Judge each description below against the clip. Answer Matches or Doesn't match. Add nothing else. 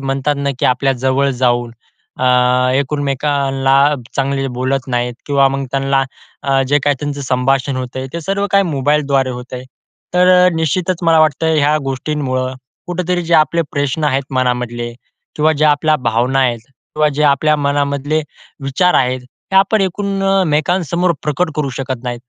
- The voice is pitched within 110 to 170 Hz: Matches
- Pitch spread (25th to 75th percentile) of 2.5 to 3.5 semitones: Matches